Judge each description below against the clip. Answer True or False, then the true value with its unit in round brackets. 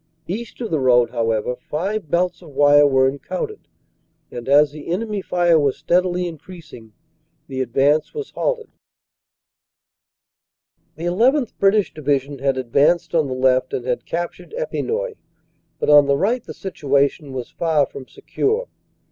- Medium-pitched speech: True (150 Hz)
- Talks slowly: False (145 wpm)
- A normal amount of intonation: False (5.9 semitones)